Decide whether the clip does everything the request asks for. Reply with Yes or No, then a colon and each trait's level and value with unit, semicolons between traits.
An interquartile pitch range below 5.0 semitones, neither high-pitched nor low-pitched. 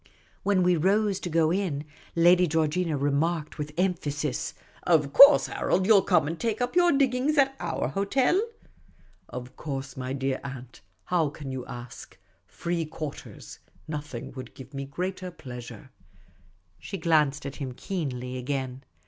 No: average, 5.3 semitones; medium, 155 Hz